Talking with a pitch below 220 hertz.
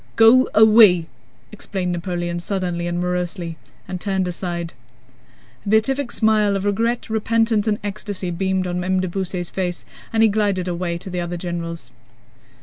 Yes: medium, 185 Hz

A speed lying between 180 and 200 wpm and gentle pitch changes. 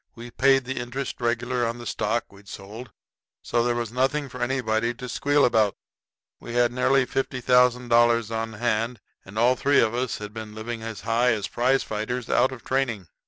Yes: average, 185 wpm; narrow, 2.1 semitones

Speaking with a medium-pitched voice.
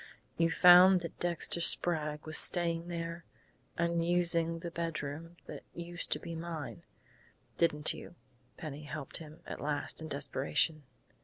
Yes: medium, 165 Hz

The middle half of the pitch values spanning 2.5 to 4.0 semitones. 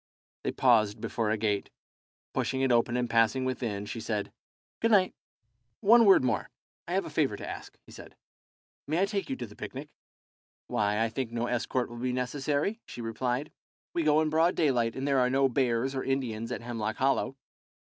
Yes: average, 3.2 semitones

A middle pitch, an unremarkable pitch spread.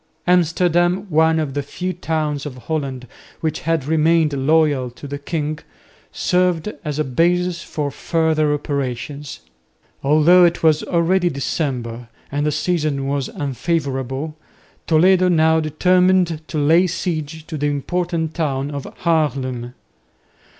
Yes: medium, 155 Hz; average, 3.1 semitones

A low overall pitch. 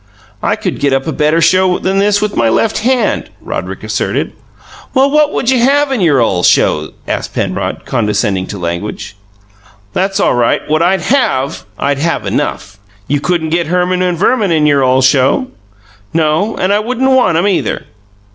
No: medium, 170 Hz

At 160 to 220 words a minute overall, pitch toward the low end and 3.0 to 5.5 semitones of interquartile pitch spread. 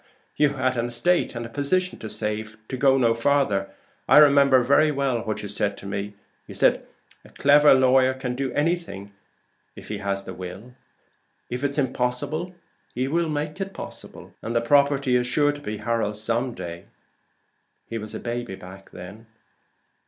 Yes: average, 165 wpm; low, 125 Hz; average, 4.7 semitones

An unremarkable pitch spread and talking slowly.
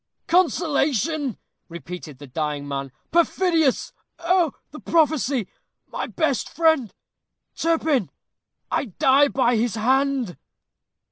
No: wide, 7.3 semitones; slow, 95 wpm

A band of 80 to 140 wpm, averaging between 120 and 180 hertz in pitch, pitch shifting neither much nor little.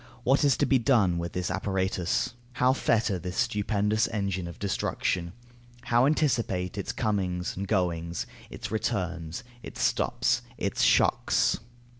No: slow, 135 wpm; low, 100 Hz; average, 4.3 semitones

